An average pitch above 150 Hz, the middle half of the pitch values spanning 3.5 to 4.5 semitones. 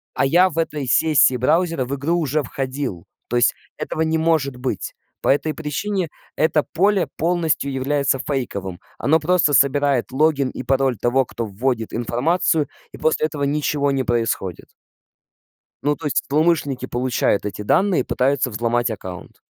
No: medium, 140 Hz; average, 4.0 semitones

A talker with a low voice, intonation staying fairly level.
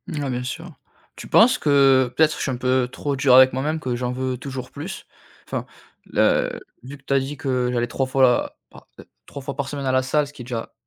Yes: low, 130 Hz; narrow, 1.9 semitones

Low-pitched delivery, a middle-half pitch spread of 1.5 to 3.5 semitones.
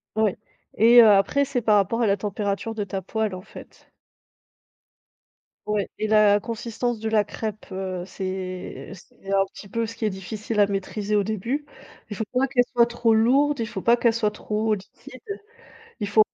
No: high, 215 Hz; narrow, 2.6 semitones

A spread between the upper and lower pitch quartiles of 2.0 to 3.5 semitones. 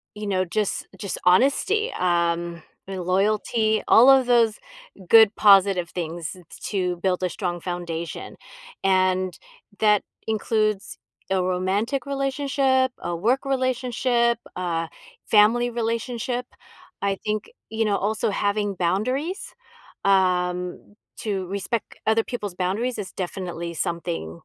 No: average, 4.4 semitones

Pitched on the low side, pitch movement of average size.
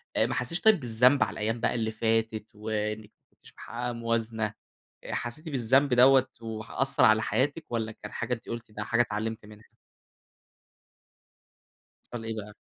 No: low, 115 Hz; narrow, 2.1 semitones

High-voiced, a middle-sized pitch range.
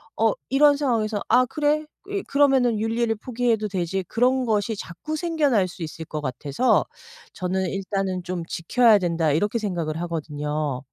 No: high, 210 Hz; wide, 6.6 semitones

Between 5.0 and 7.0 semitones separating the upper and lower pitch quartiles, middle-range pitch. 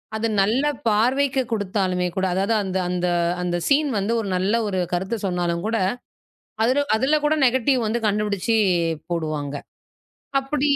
No: wide, 5.4 semitones; high, 210 Hz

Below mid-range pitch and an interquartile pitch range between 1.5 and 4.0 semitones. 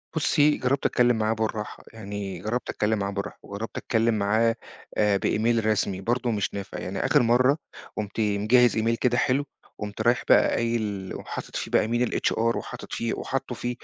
Yes: low, 110 Hz; average, 2.8 semitones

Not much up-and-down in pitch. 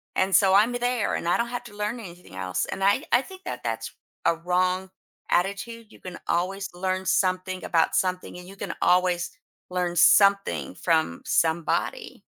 Yes: narrow, 2.3 semitones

